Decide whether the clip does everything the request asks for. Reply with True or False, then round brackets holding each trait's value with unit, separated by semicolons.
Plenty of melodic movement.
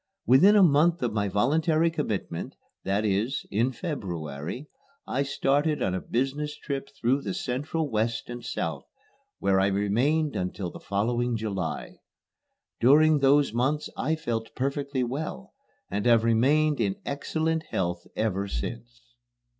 True (6.2 semitones)